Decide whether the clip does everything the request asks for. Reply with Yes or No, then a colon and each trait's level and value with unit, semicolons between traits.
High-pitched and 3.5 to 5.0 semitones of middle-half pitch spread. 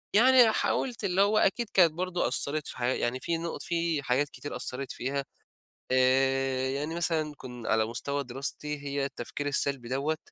No: medium, 140 Hz; average, 4.3 semitones